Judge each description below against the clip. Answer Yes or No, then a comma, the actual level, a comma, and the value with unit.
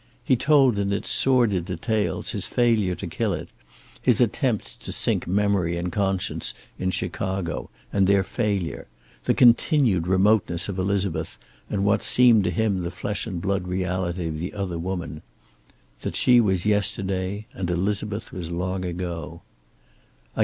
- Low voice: Yes, very low, 95 Hz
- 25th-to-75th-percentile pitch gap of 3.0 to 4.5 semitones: No, narrow, 2.6 semitones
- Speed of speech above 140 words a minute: Yes, average, 150 wpm